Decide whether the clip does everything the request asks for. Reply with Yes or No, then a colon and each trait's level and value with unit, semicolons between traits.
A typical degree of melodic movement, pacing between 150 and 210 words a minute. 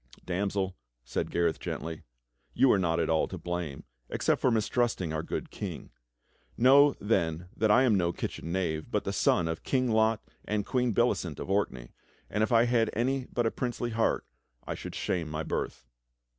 No: wide, 6.0 semitones; average, 180 wpm